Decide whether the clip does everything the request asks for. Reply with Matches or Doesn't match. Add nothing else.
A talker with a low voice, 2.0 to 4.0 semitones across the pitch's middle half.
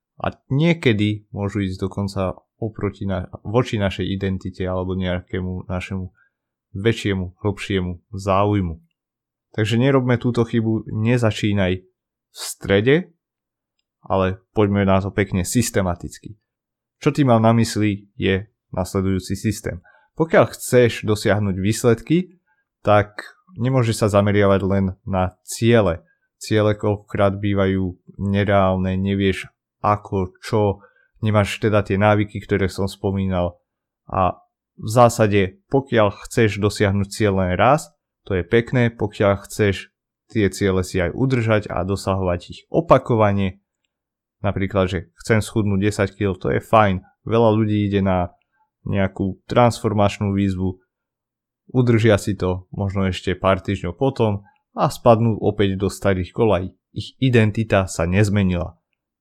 Matches